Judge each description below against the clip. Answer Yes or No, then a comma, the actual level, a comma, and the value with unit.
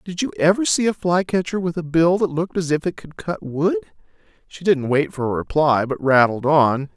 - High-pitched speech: No, medium, 160 Hz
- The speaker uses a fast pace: Yes, fast, 225 wpm